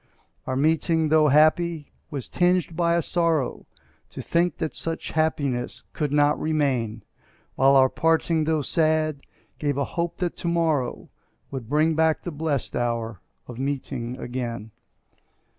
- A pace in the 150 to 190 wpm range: No, average, 140 wpm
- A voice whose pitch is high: No, medium, 150 Hz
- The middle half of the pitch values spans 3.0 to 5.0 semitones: Yes, average, 3.7 semitones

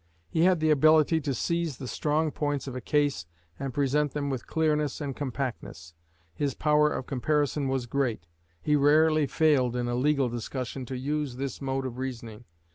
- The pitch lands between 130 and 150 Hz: Yes, medium, 140 Hz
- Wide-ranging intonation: No, average, 2.8 semitones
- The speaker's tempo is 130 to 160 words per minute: No, average, 180 wpm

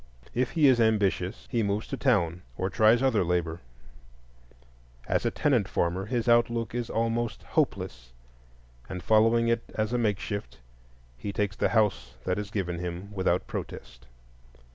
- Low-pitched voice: Yes, low, 105 Hz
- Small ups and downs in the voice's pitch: No, average, 4.2 semitones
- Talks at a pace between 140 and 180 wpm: Yes, average, 150 wpm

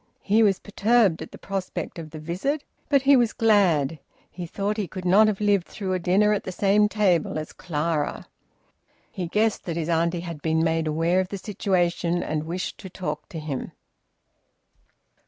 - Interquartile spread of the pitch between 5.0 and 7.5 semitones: No, average, 3.9 semitones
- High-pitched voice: No, medium, 180 Hz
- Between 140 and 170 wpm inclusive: No, average, 185 wpm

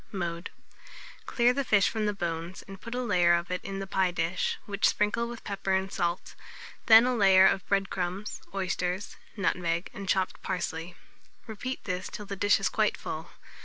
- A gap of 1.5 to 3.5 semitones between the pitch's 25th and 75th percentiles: Yes, narrow, 2.6 semitones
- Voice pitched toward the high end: Yes, high, 195 Hz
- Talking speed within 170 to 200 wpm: Yes, average, 185 wpm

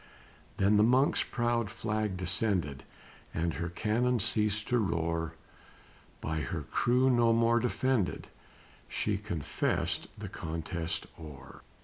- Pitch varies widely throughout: Yes, wide, 5.9 semitones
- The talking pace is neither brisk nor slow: No, slow, 115 wpm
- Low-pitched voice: Yes, low, 105 Hz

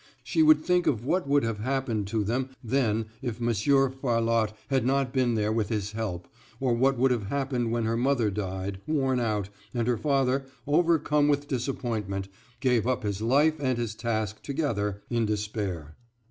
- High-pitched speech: No, low, 120 Hz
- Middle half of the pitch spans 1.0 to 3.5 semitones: No, average, 4.1 semitones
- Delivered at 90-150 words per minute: No, average, 175 wpm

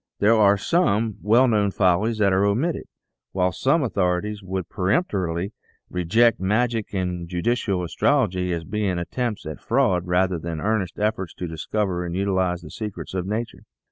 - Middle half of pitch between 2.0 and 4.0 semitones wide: Yes, average, 3.5 semitones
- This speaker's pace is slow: No, average, 160 wpm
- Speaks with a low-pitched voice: Yes, low, 100 Hz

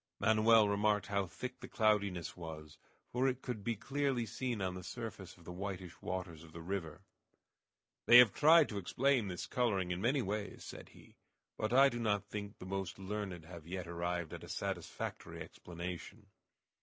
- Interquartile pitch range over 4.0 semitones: Yes, average, 4.7 semitones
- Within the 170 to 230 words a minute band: Yes, average, 180 wpm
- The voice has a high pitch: No, low, 100 Hz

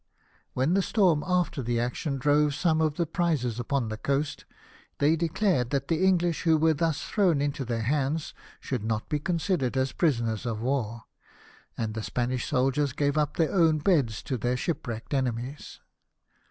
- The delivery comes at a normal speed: Yes, average, 170 wpm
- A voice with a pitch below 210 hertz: Yes, medium, 140 Hz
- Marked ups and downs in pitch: No, average, 4.8 semitones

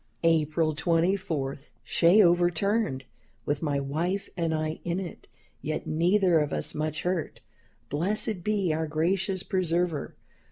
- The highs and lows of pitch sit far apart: No, average, 3.2 semitones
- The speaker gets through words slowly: Yes, slow, 125 wpm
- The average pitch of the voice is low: No, medium, 170 Hz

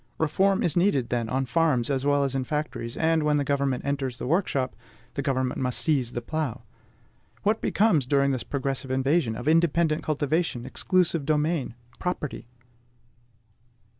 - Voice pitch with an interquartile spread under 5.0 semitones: Yes, average, 3.6 semitones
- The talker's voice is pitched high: No, medium, 140 Hz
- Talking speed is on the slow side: No, average, 155 wpm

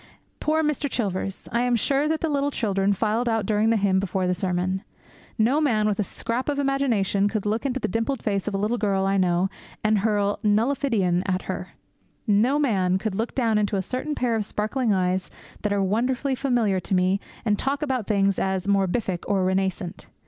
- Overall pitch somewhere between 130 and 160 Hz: No, high, 210 Hz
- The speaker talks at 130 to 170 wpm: No, average, 200 wpm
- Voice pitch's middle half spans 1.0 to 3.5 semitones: No, average, 4.2 semitones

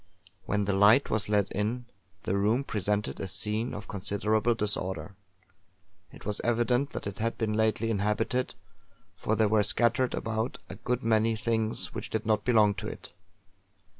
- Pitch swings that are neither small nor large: No, narrow, 1.9 semitones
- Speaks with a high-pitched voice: No, low, 110 Hz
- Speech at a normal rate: Yes, average, 165 wpm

